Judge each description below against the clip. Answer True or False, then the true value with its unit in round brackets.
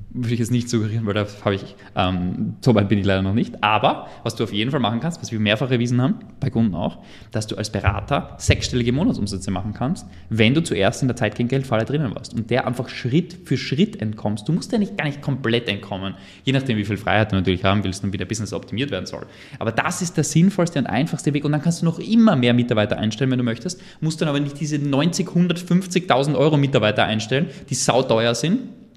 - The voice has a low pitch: True (120 Hz)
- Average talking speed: False (235 wpm)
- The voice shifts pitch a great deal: True (6.0 semitones)